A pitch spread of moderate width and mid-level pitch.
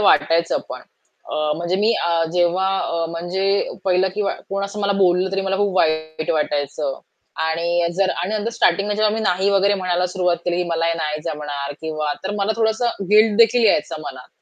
Yes: average, 3.5 semitones; medium, 180 Hz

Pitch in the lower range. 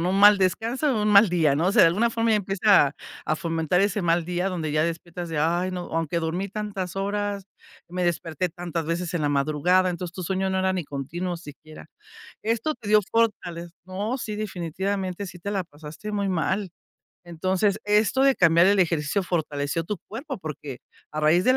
No: medium, 180 Hz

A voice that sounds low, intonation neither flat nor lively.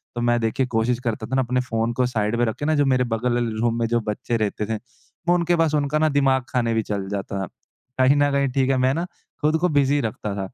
Yes: low, 125 Hz; average, 3.7 semitones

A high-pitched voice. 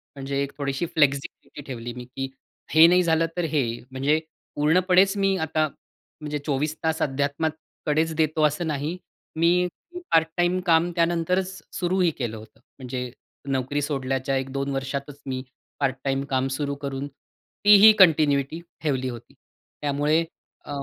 No: medium, 145 Hz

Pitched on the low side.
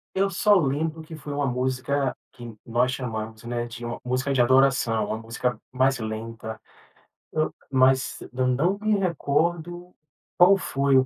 Yes: low, 130 Hz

